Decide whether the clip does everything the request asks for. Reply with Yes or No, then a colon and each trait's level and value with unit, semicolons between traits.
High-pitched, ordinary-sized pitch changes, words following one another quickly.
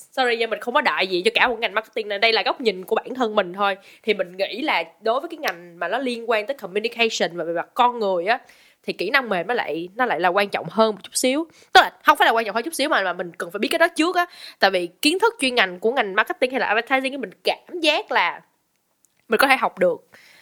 No: high, 235 Hz; wide, 6.9 semitones; fast, 285 wpm